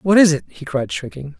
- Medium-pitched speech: Yes, medium, 155 Hz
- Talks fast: Yes, fast, 260 wpm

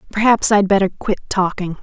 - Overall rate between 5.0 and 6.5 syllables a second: Yes, 5.6 syllables/s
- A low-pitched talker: No, high, 195 Hz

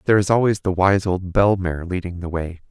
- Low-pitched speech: Yes, very low, 95 Hz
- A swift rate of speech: Yes, fast, 245 wpm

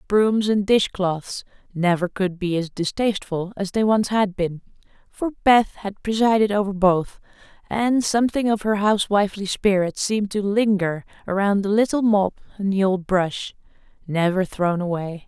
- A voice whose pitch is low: No, high, 200 Hz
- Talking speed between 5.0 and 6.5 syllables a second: No, 4.7 syllables/s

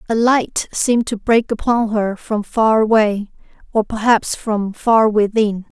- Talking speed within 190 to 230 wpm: No, average, 145 wpm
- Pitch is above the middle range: Yes, high, 220 Hz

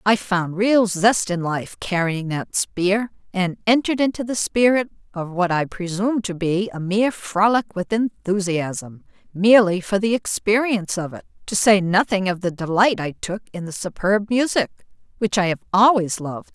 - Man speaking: No, female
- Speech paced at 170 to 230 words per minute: Yes, average, 175 wpm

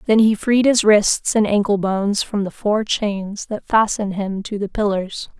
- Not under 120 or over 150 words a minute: No, average, 200 wpm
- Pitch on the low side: No, high, 205 Hz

